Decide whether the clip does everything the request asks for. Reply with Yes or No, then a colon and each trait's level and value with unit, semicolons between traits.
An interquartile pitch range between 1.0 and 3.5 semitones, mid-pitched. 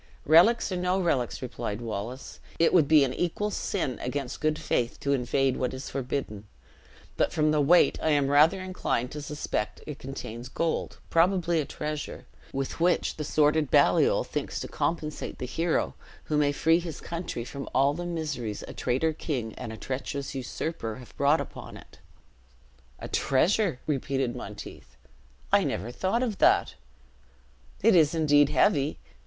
No: average, 4.2 semitones; medium, 145 Hz